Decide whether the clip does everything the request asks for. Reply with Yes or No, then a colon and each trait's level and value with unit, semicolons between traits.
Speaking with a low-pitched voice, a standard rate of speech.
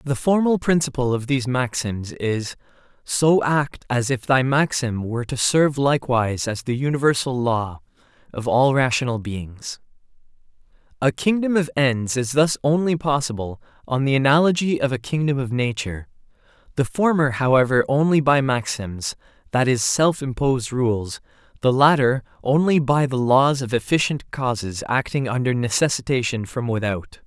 Yes: low, 130 Hz; average, 145 wpm